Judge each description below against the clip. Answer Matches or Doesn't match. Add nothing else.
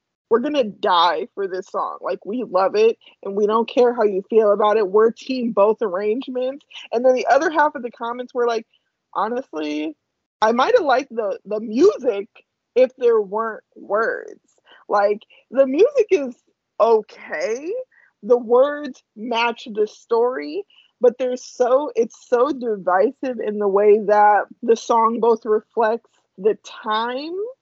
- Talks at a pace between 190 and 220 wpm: Doesn't match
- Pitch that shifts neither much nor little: Doesn't match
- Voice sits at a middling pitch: Doesn't match